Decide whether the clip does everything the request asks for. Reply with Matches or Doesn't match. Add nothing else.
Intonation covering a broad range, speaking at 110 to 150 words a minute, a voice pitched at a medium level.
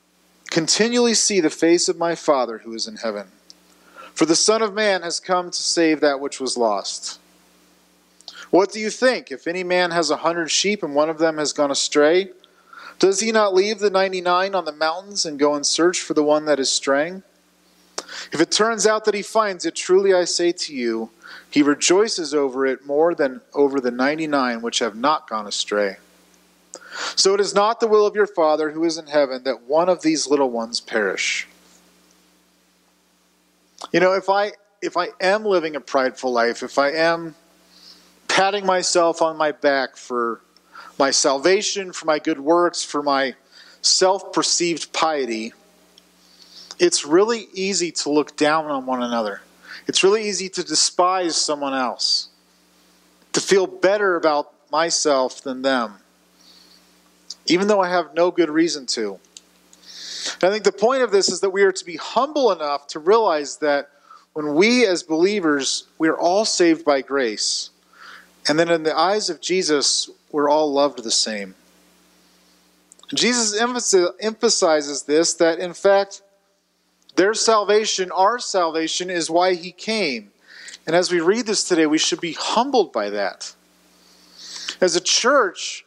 Doesn't match